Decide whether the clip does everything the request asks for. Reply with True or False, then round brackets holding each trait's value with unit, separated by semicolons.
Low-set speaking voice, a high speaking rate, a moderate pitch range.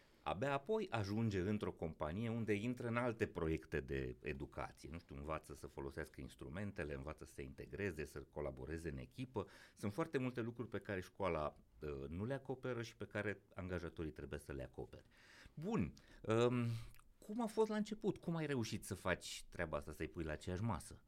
False (100 Hz; 180 wpm; 7.6 semitones)